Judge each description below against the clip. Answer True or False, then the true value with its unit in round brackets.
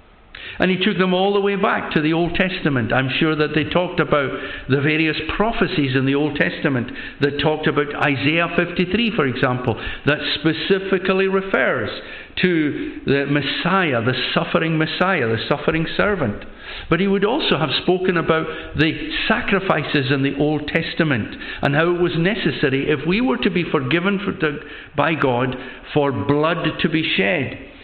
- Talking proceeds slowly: False (165 wpm)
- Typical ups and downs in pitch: True (4.1 semitones)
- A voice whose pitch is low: False (160 Hz)